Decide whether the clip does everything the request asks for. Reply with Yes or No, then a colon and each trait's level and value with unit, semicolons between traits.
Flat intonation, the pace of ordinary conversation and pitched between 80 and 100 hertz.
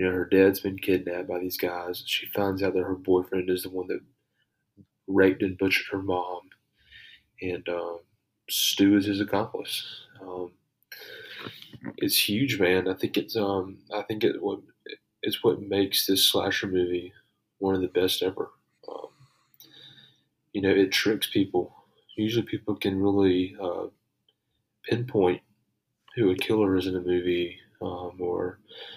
Yes: narrow, 1.4 semitones; average, 155 wpm; very low, 95 Hz